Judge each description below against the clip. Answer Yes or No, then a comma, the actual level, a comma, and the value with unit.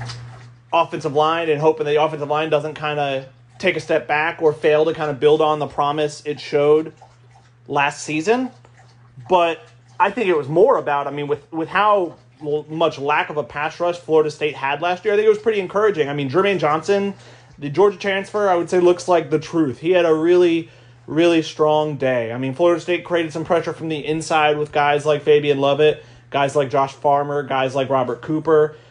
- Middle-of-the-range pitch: Yes, medium, 150 Hz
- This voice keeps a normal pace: No, fast, 210 wpm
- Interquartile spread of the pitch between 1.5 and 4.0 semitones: Yes, average, 2.8 semitones